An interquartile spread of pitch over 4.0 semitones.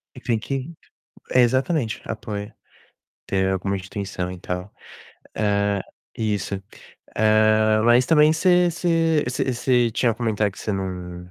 Yes: average, 4.4 semitones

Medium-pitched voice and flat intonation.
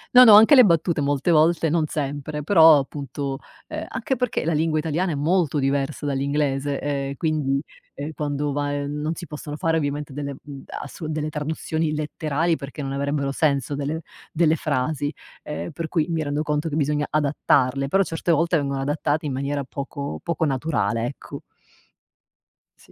Yes: medium, 150 Hz; narrow, 2.3 semitones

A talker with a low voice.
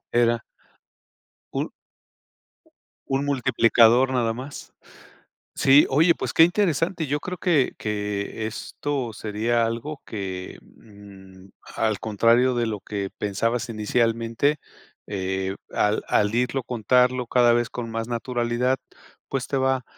Yes: low, 120 Hz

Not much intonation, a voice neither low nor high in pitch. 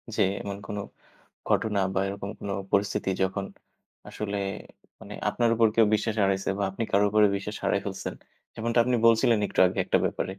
No: narrow, 2.2 semitones; low, 105 Hz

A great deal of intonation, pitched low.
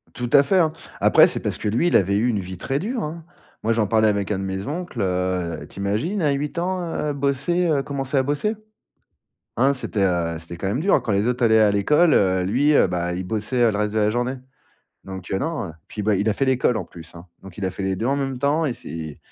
Yes: wide, 6.6 semitones; low, 110 Hz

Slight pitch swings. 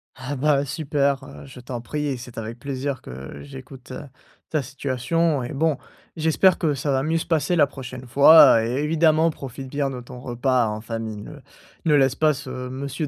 No: average, 3.1 semitones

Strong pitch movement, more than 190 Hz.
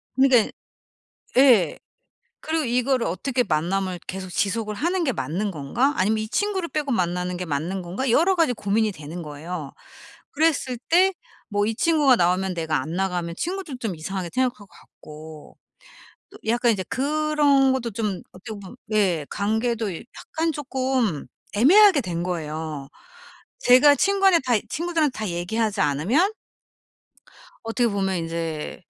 Yes: wide, 7.3 semitones; high, 215 Hz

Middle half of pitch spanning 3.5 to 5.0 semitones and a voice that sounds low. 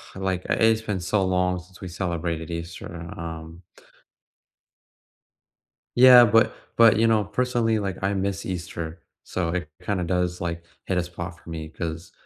No: average, 2.9 semitones; very low, 90 Hz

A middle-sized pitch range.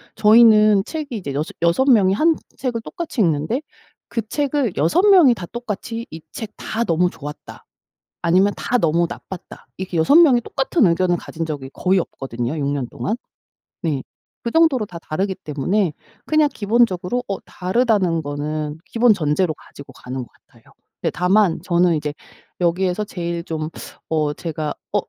No: wide, 6.5 semitones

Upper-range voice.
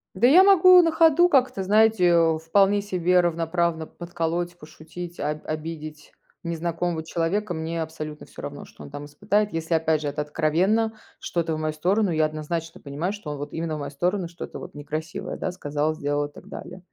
No: medium, 165 Hz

